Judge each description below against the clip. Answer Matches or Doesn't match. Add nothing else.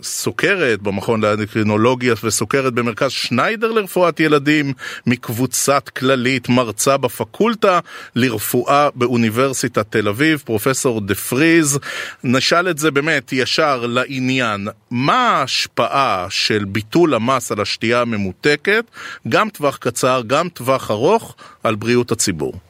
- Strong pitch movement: Doesn't match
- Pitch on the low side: Matches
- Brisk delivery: Doesn't match